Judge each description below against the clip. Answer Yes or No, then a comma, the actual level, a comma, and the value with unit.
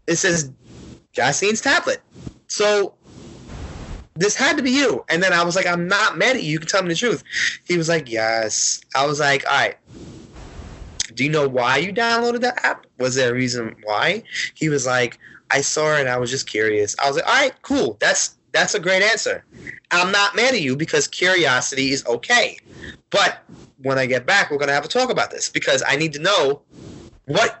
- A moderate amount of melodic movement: No, wide, 7.9 semitones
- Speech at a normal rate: No, fast, 210 wpm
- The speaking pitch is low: No, medium, 150 Hz